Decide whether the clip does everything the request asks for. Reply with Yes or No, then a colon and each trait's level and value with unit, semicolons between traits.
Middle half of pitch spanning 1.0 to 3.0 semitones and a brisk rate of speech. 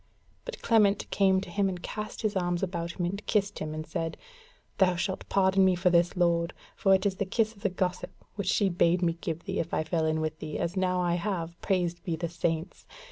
Yes: narrow, 2.5 semitones; fast, 235 wpm